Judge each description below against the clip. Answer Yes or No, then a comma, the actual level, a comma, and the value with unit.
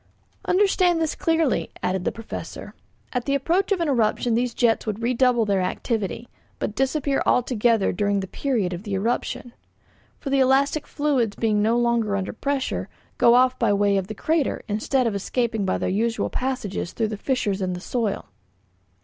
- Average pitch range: Yes, average, 4.6 semitones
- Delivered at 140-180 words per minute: Yes, average, 175 wpm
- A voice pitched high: Yes, high, 235 Hz